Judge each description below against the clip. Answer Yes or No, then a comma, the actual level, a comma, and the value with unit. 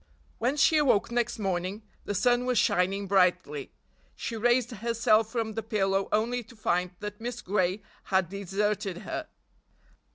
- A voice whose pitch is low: No, high, 210 Hz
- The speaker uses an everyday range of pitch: Yes, average, 3.6 semitones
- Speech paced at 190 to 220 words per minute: No, average, 150 wpm